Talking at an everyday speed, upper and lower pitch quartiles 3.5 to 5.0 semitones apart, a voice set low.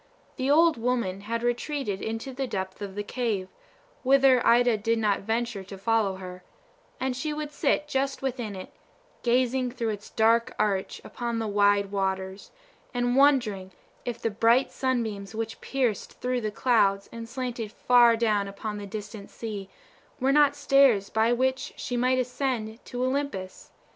No: average, 160 wpm; average, 3.8 semitones; high, 230 Hz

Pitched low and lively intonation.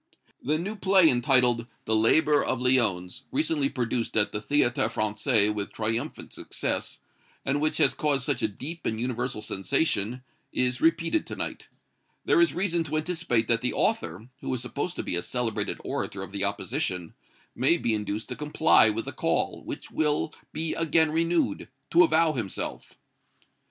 Yes: low, 125 Hz; wide, 6.1 semitones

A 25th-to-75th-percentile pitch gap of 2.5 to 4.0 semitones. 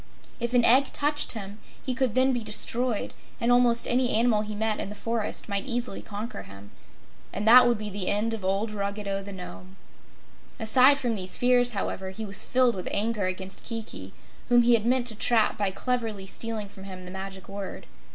Yes: average, 3.6 semitones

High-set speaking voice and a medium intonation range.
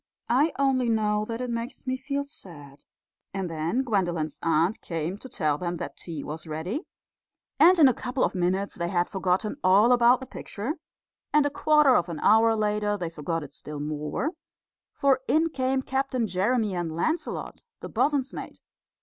No: high, 210 Hz; wide, 7.2 semitones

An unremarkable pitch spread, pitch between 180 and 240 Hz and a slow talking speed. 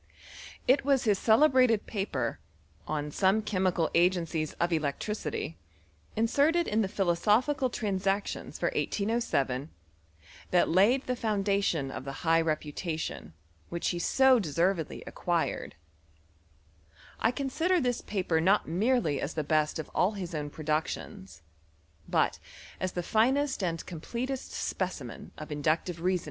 No: wide, 6.1 semitones; medium, 185 Hz; slow, 120 wpm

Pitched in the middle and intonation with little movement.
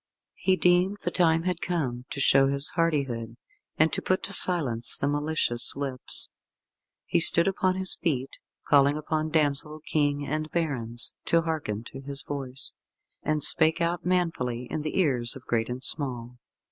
No: medium, 145 Hz; average, 4.3 semitones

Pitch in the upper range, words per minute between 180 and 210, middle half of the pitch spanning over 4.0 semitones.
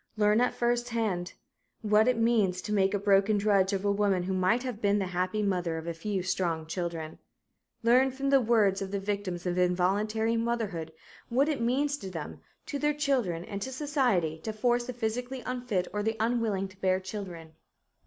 Yes: high, 210 Hz; average, 195 wpm; average, 4.4 semitones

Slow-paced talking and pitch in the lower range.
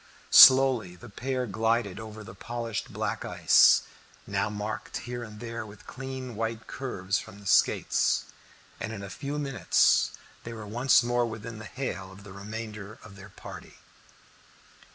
No: average, 155 wpm; low, 110 Hz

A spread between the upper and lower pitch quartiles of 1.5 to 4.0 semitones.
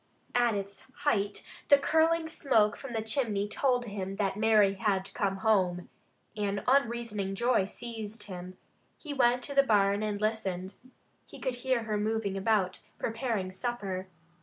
Yes: average, 3.4 semitones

